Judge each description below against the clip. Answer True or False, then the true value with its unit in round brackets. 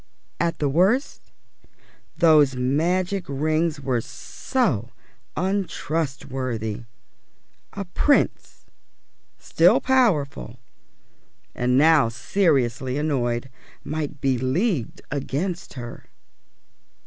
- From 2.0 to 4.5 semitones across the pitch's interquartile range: False (5.1 semitones)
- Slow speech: True (75 wpm)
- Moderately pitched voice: True (145 Hz)